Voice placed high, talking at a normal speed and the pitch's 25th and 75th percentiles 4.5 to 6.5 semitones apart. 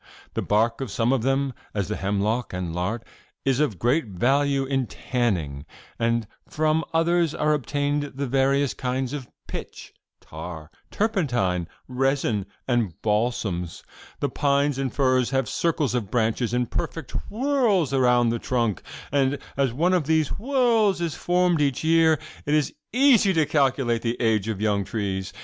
No: low, 130 Hz; average, 155 wpm; average, 5.1 semitones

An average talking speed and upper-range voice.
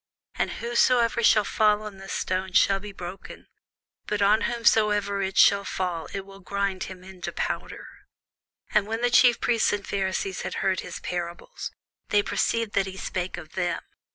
Yes: average, 170 wpm; high, 200 Hz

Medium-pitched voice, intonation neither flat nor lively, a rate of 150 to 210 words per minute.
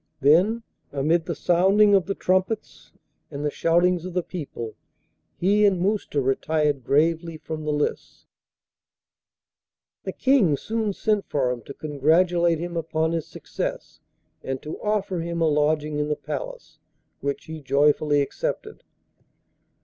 No: medium, 165 Hz; average, 4.0 semitones; average, 140 wpm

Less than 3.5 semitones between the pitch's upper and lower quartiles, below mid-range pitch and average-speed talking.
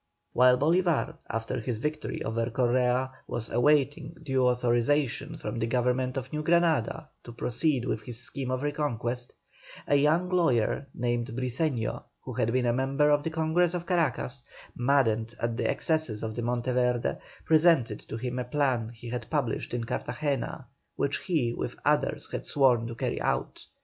No: average, 3.8 semitones; low, 130 Hz; average, 160 wpm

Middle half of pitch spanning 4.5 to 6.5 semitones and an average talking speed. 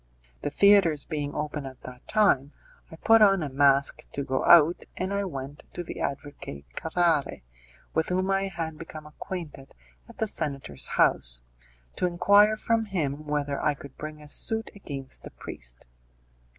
Yes: average, 5.0 semitones; average, 165 wpm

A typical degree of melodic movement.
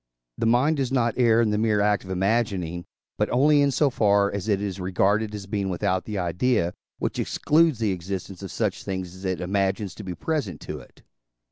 Yes: average, 3.7 semitones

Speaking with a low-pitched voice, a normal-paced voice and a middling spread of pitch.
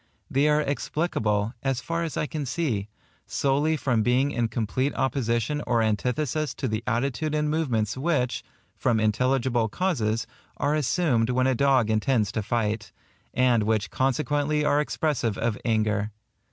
Yes: low, 125 Hz; average, 150 wpm; average, 4.7 semitones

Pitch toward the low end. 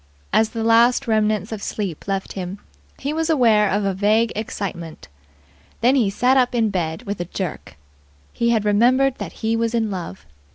No: high, 215 Hz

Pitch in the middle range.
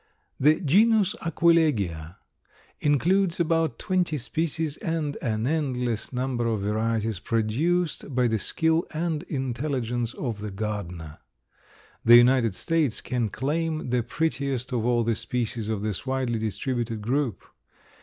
No: low, 125 Hz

